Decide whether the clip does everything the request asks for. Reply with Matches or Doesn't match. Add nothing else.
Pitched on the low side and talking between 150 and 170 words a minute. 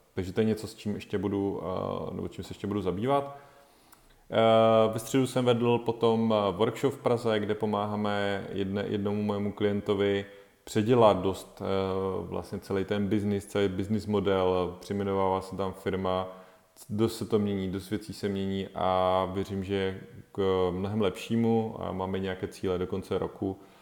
Matches